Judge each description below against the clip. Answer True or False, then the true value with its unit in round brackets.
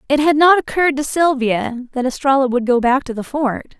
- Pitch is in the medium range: False (270 Hz)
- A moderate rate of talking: False (220 wpm)